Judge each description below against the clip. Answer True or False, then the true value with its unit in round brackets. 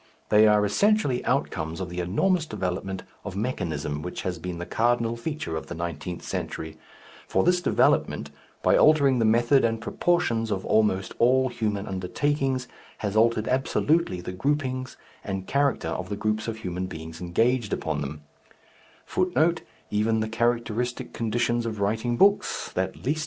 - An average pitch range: False (6.2 semitones)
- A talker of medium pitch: False (110 Hz)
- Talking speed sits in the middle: False (130 wpm)